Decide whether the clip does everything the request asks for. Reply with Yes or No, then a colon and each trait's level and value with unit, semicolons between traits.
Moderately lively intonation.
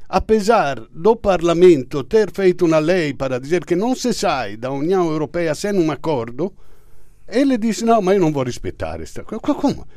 No: wide, 6.9 semitones